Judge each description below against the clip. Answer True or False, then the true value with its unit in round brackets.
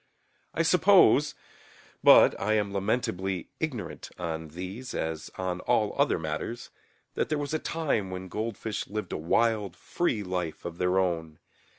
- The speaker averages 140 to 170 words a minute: True (150 wpm)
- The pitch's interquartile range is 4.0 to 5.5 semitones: True (4.4 semitones)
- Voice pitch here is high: False (95 Hz)